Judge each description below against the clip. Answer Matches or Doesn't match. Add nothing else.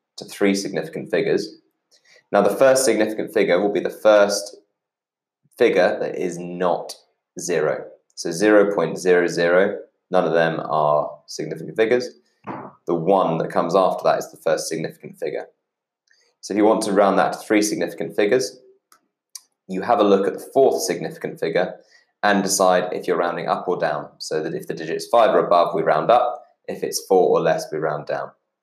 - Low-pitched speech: Matches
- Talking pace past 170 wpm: Matches